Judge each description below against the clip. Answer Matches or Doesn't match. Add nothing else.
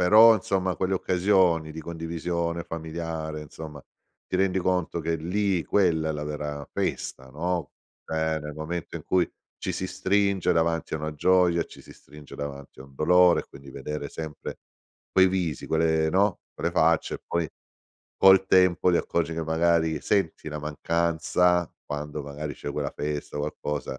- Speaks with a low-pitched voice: Matches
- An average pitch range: Matches